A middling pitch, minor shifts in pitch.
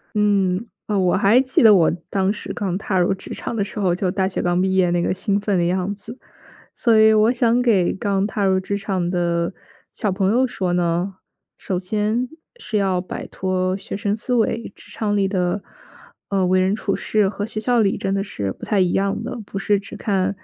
No: high, 195 Hz; narrow, 2.3 semitones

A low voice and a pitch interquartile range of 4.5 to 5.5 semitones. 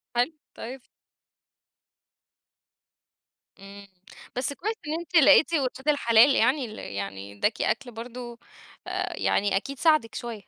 No: high, 245 Hz; average, 4.8 semitones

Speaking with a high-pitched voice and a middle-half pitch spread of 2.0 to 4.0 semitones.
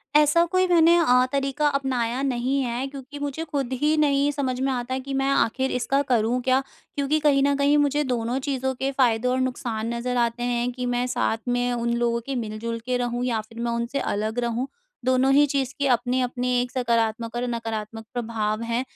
Yes: very high, 250 Hz; average, 2.7 semitones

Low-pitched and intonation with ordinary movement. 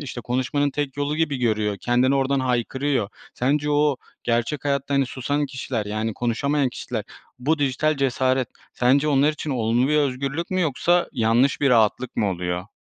Yes: low, 130 Hz; average, 3.1 semitones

